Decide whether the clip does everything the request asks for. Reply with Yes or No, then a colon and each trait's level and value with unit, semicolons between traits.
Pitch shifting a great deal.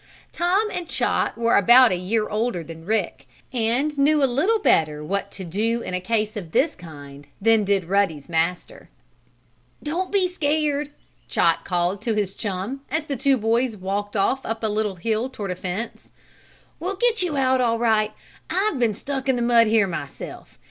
Yes: wide, 6.0 semitones